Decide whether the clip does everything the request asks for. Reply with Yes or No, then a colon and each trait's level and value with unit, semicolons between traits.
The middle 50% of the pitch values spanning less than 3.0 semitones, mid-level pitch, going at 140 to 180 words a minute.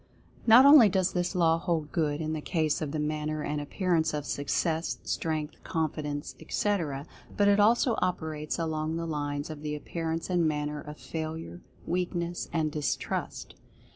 Yes: narrow, 2.5 semitones; medium, 160 Hz; average, 165 wpm